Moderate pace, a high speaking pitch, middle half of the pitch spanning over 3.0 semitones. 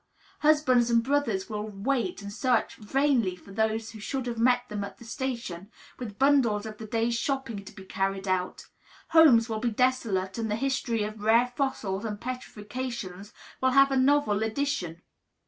Yes: average, 175 wpm; high, 230 Hz; average, 3.9 semitones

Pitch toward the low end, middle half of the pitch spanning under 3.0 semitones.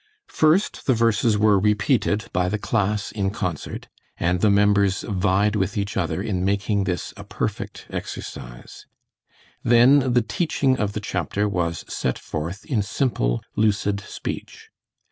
Yes: low, 105 Hz; narrow, 2.5 semitones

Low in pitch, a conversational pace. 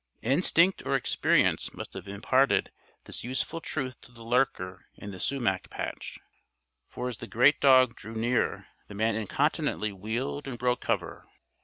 Yes: low, 120 Hz; average, 155 wpm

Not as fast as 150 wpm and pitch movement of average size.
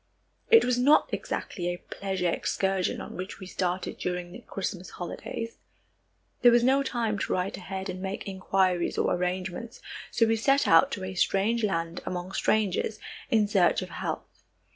No: average, 165 wpm; average, 3.8 semitones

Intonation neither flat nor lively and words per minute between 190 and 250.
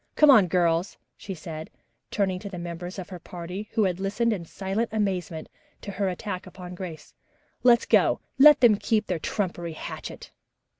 No: average, 3.3 semitones; average, 180 wpm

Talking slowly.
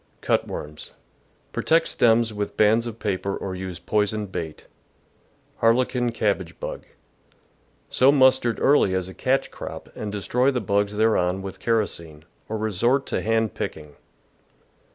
No: average, 145 wpm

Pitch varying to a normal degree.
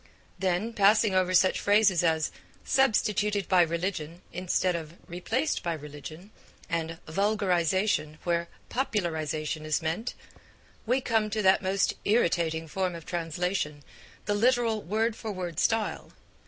Yes: average, 4.2 semitones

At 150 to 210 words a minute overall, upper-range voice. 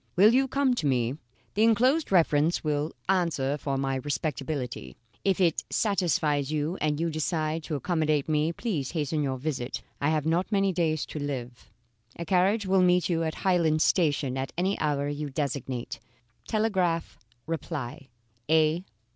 No: average, 155 wpm; medium, 155 Hz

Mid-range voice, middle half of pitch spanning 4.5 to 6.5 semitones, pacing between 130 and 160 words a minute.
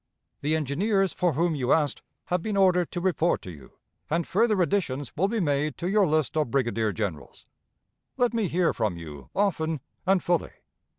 No: medium, 165 Hz; wide, 5.6 semitones; average, 180 wpm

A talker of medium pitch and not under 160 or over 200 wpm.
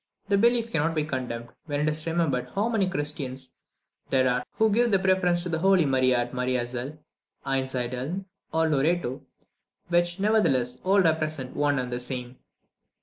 Yes: medium, 150 Hz; average, 165 wpm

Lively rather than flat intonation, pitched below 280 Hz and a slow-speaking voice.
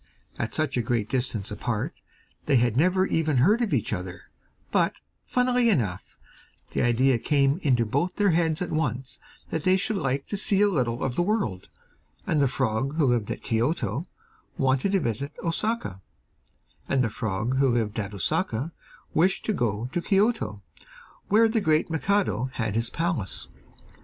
No: wide, 7.4 semitones; medium, 140 Hz; average, 165 wpm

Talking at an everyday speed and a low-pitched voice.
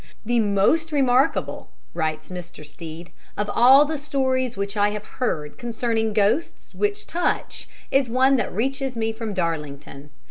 No: average, 145 wpm; high, 225 Hz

